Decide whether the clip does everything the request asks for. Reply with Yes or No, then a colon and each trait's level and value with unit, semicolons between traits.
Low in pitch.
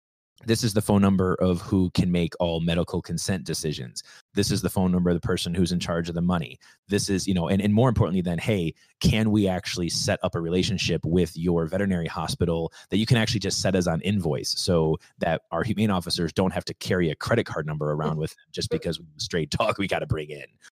Yes: very low, 90 Hz